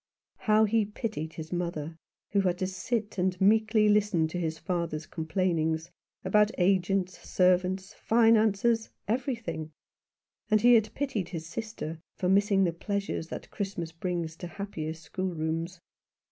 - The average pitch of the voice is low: No, medium, 185 Hz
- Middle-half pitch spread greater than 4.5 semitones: No, average, 4.0 semitones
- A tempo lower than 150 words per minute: Yes, average, 140 wpm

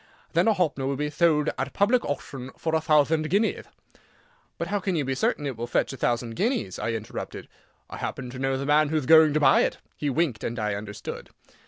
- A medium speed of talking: No, fast, 220 wpm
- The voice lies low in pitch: No, medium, 145 Hz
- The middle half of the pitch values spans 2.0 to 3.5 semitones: No, average, 4.1 semitones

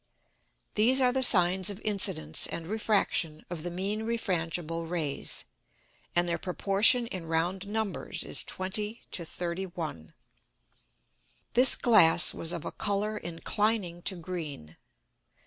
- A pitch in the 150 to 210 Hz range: Yes, medium, 185 Hz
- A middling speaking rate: No, slow, 125 wpm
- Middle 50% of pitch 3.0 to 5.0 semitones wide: Yes, average, 4.1 semitones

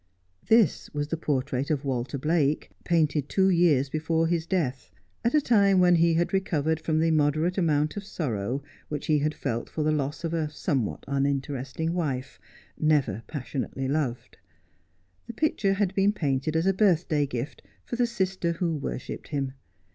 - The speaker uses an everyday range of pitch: Yes, average, 3.8 semitones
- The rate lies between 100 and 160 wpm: No, average, 170 wpm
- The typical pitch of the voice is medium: Yes, medium, 155 Hz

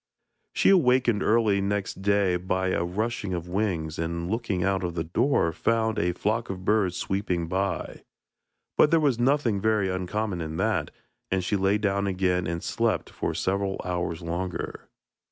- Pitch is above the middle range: No, very low, 95 Hz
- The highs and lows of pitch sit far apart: No, average, 3.3 semitones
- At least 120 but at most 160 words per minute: No, average, 170 wpm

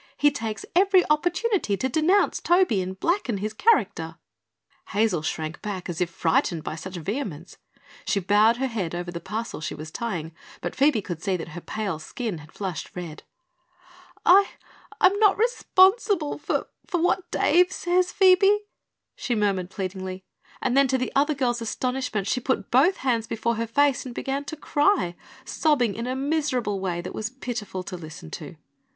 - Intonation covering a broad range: Yes, wide, 8.3 semitones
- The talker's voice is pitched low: No, high, 230 Hz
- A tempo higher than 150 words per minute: Yes, average, 170 wpm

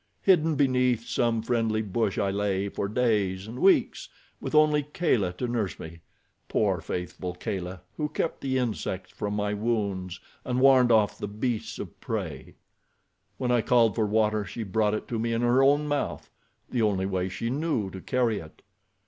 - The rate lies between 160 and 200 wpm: Yes, average, 170 wpm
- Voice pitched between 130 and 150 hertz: No, low, 110 Hz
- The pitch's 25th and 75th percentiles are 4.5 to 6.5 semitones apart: No, average, 4.1 semitones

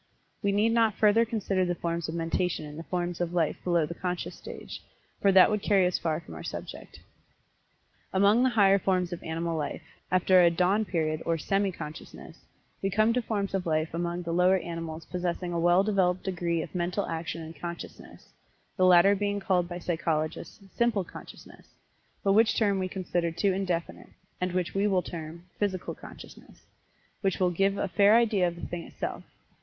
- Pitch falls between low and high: Yes, medium, 180 Hz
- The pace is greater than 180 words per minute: Yes, average, 190 wpm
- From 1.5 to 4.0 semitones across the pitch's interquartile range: Yes, average, 2.7 semitones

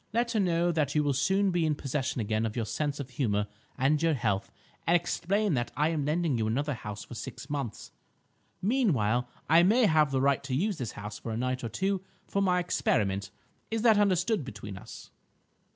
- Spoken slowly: No, fast, 205 wpm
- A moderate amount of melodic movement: No, wide, 6.9 semitones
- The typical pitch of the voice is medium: Yes, medium, 145 Hz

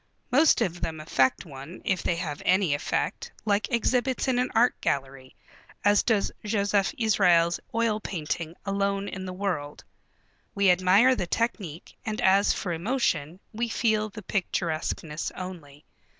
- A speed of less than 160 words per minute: Yes, average, 145 wpm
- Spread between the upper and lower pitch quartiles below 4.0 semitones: No, average, 4.6 semitones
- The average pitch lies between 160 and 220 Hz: Yes, high, 190 Hz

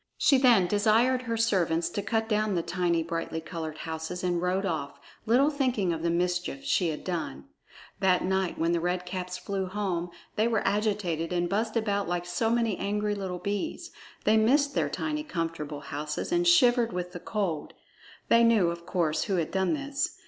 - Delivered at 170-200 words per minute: Yes, average, 185 wpm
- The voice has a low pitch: No, high, 190 Hz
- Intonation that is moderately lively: Yes, average, 4.6 semitones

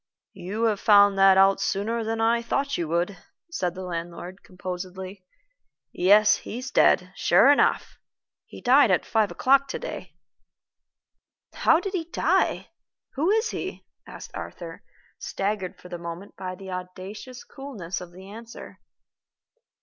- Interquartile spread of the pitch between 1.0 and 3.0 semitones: No, average, 4.2 semitones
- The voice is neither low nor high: No, high, 195 Hz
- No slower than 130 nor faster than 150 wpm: Yes, average, 140 wpm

